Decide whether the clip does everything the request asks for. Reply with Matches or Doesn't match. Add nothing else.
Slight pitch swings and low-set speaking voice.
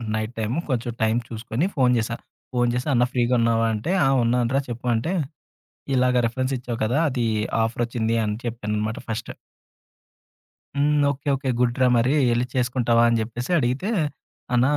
Matches